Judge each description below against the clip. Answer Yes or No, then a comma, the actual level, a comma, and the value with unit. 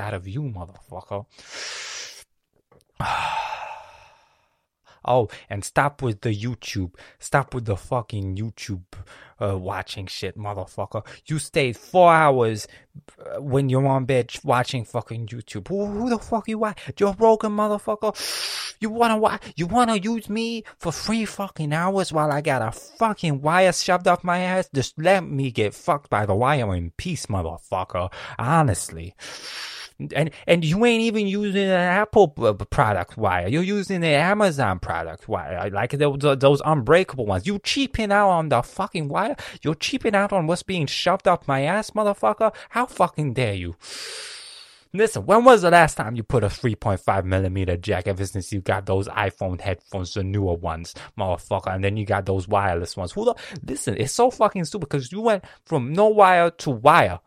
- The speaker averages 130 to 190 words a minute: Yes, average, 170 wpm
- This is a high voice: No, medium, 140 Hz